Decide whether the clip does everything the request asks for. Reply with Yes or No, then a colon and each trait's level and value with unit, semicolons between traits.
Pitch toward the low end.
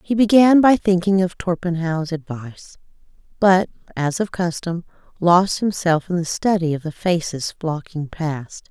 No: medium, 175 Hz